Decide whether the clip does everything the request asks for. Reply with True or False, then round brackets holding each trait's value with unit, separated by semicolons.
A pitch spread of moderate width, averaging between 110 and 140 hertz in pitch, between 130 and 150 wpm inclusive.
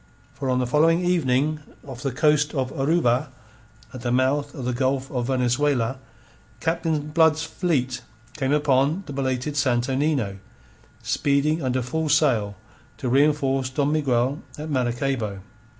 True (3.0 semitones; 135 Hz; 140 wpm)